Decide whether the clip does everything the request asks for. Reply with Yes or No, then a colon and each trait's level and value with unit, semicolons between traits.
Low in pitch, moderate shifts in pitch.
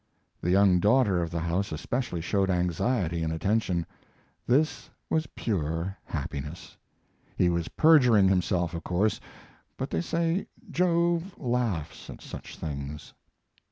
No: very low, 95 Hz; wide, 6.8 semitones